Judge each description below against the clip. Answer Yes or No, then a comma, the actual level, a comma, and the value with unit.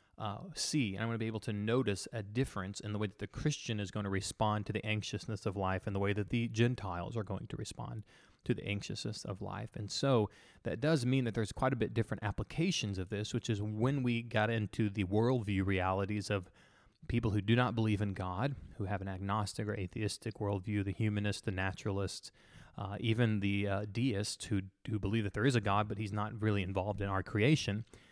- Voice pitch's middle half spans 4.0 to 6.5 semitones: No, narrow, 2.4 semitones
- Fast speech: Yes, fast, 225 wpm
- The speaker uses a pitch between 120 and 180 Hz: No, low, 105 Hz